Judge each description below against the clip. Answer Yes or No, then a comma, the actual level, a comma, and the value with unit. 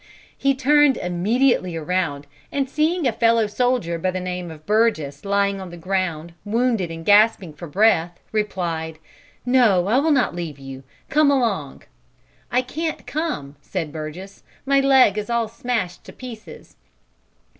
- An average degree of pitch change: No, wide, 6.5 semitones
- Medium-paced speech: Yes, average, 150 wpm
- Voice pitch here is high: Yes, high, 200 Hz